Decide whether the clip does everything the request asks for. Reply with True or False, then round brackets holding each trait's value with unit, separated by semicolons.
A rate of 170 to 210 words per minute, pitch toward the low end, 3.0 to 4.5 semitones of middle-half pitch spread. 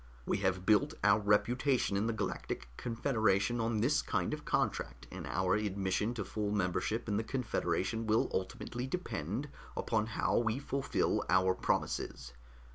False (150 wpm; 110 Hz; 3.7 semitones)